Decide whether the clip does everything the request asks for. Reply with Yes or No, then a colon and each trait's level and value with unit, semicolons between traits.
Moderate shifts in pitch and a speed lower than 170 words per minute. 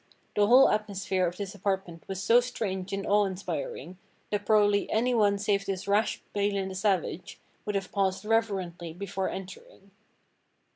No: narrow, 1.7 semitones; average, 150 wpm